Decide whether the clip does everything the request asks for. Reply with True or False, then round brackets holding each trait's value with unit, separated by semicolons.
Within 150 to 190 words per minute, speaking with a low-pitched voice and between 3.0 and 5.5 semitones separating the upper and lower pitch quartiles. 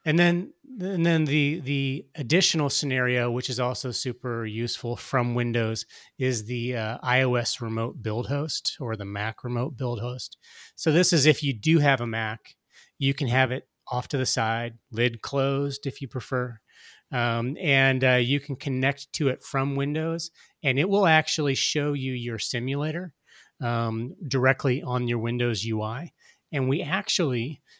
True (165 wpm; 130 Hz; 3.3 semitones)